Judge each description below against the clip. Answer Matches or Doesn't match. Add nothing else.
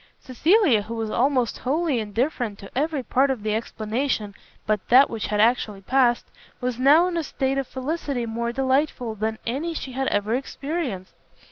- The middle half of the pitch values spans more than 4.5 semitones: Doesn't match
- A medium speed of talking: Matches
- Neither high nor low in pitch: Doesn't match